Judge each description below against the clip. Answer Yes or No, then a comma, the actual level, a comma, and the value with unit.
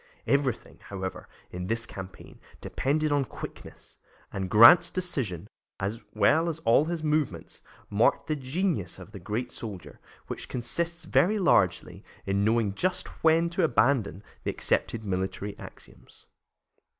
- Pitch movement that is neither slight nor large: No, wide, 8.0 semitones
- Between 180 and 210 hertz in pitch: No, low, 115 Hz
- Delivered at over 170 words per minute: No, slow, 135 wpm